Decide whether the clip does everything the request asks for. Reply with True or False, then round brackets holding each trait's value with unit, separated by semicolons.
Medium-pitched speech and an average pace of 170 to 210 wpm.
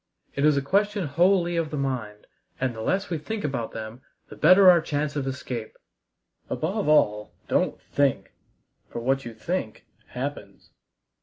False (145 Hz; 160 wpm)